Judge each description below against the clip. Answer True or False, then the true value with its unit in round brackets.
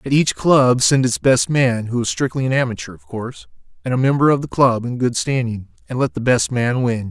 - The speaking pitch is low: True (125 Hz)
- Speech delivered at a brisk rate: True (245 wpm)